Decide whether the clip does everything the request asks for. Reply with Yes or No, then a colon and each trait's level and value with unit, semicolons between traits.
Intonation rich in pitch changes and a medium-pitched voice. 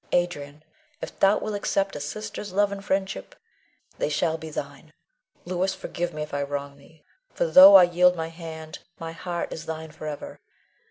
No: average, 3.9 semitones; medium, 165 Hz